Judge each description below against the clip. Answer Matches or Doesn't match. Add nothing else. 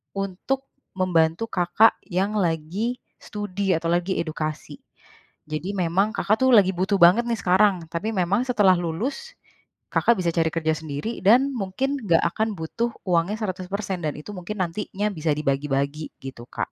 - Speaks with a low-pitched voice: Doesn't match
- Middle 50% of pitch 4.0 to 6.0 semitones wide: Matches